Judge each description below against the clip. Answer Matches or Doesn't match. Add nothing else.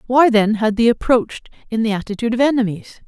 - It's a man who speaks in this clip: Doesn't match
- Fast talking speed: Doesn't match